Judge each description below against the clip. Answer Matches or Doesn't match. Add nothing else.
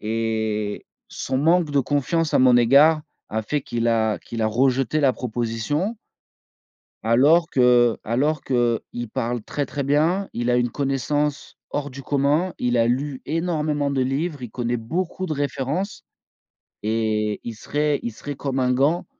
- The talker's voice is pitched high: Doesn't match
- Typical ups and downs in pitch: Matches